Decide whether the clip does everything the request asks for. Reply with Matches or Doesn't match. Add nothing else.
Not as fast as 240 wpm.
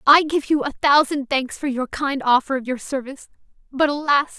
Matches